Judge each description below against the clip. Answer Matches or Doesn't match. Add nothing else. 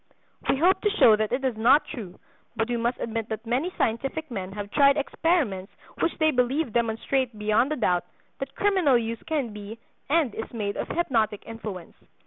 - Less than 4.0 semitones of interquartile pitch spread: Doesn't match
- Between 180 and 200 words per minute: Matches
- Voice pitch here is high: Matches